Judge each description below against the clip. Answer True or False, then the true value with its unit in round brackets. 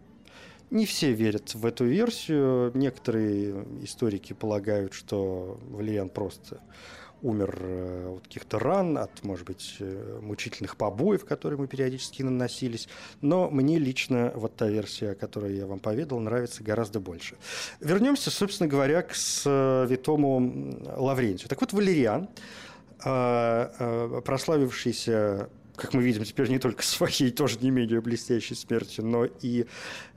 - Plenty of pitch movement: False (4.4 semitones)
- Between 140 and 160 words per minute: False (125 wpm)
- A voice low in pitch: True (120 Hz)